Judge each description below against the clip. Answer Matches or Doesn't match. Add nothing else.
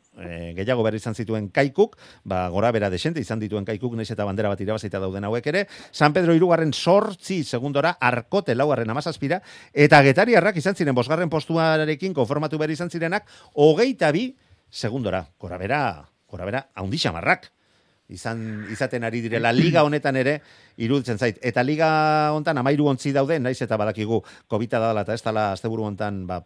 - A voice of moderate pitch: Doesn't match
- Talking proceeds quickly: Doesn't match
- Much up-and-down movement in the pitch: Matches